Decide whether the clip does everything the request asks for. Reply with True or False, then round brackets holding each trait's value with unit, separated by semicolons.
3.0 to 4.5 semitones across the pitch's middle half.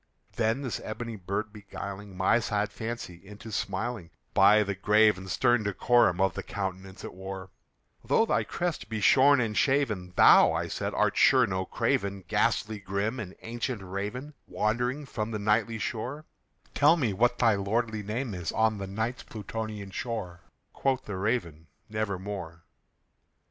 True (3.4 semitones)